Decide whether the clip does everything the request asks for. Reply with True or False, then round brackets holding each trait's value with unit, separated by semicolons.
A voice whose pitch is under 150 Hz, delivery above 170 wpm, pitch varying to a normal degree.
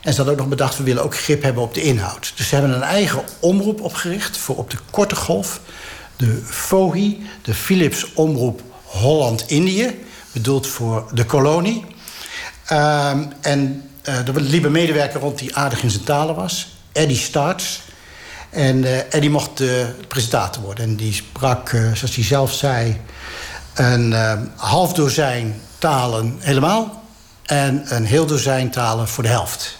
False (140 Hz; 165 wpm; 4.5 semitones)